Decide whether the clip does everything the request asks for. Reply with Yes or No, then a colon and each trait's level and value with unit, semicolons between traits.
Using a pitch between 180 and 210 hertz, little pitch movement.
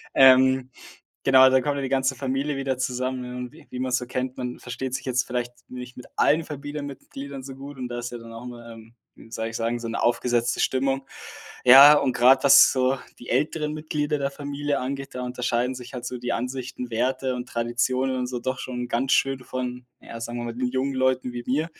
No: low, 130 Hz; narrow, 1.6 semitones